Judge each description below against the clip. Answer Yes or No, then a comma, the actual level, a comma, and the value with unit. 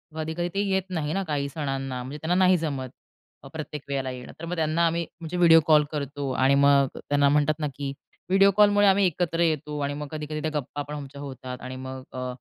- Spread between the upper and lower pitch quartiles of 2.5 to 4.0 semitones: Yes, average, 3.1 semitones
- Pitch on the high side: No, medium, 150 Hz